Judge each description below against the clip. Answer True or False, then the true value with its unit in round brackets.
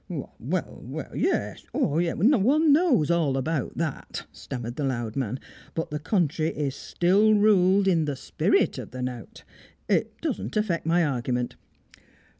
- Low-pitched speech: False (160 Hz)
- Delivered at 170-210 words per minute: False (145 wpm)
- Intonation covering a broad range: True (6.4 semitones)